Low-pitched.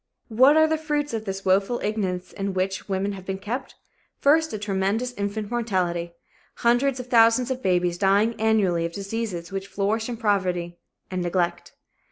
No: high, 205 Hz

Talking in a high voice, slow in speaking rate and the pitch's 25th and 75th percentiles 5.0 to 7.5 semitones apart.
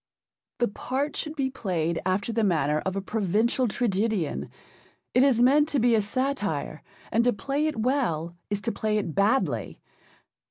No: high, 220 Hz; average, 165 wpm; wide, 5.5 semitones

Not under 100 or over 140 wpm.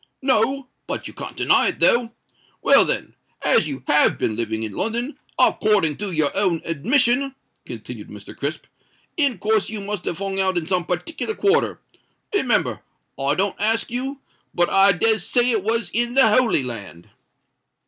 No: average, 160 wpm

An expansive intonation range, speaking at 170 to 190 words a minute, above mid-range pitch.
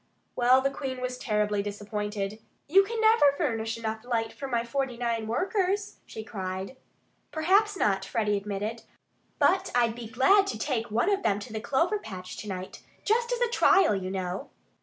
Yes: wide, 6.2 semitones; average, 180 wpm; high, 235 Hz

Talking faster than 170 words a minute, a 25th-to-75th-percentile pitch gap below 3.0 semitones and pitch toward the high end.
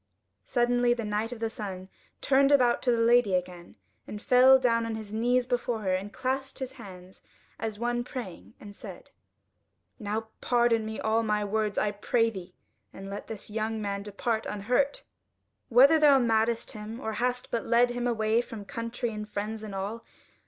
Yes: average, 180 wpm; narrow, 2.6 semitones; high, 225 Hz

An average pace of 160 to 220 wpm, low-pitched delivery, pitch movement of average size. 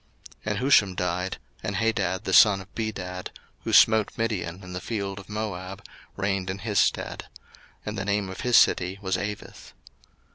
No: average, 175 wpm; low, 100 Hz; narrow, 2.3 semitones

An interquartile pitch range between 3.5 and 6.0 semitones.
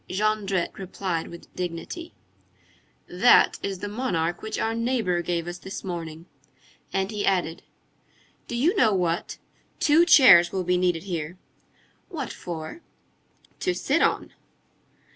Yes: average, 4.4 semitones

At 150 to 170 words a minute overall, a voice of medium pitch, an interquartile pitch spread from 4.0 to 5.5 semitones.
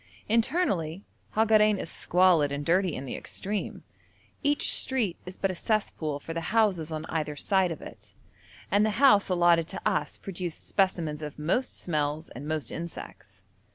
Yes: average, 160 wpm; medium, 175 Hz; average, 4.8 semitones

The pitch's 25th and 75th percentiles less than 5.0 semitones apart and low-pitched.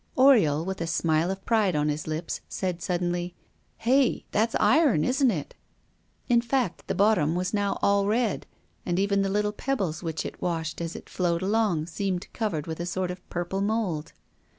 No: average, 4.2 semitones; medium, 185 Hz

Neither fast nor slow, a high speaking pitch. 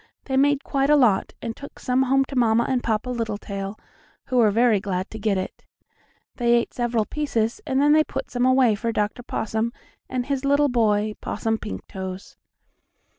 Yes: average, 175 wpm; high, 235 Hz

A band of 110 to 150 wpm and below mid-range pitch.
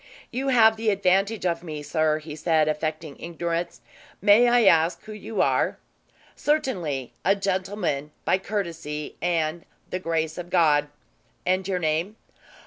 No: average, 140 wpm; medium, 175 Hz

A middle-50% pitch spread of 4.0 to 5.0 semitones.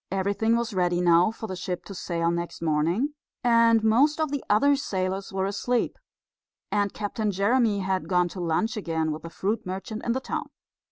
Yes: average, 4.4 semitones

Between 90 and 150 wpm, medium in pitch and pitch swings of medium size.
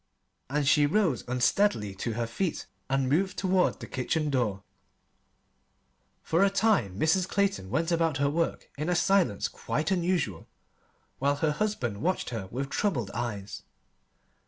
No: average, 145 wpm; medium, 150 Hz; wide, 7.4 semitones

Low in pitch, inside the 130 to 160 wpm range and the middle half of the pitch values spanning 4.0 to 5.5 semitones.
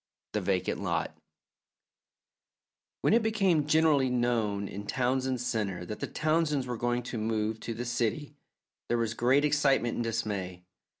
Yes: low, 120 Hz; average, 145 wpm; average, 4.6 semitones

